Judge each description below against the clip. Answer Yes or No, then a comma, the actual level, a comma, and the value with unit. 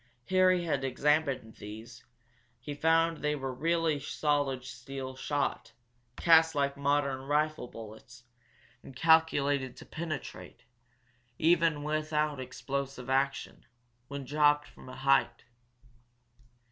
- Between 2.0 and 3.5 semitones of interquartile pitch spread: Yes, average, 2.8 semitones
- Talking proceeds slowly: Yes, slow, 110 wpm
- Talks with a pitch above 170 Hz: No, medium, 145 Hz